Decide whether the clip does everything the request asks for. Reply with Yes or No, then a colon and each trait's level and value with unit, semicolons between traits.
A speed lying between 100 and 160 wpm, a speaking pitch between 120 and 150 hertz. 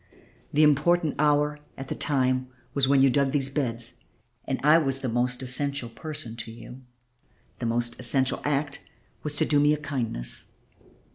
No: average, 170 wpm; low, 135 Hz